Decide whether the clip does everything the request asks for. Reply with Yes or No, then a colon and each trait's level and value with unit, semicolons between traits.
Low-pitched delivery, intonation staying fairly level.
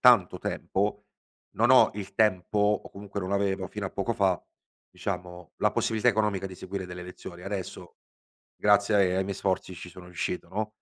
Yes: very low, 95 Hz; narrow, 2.2 semitones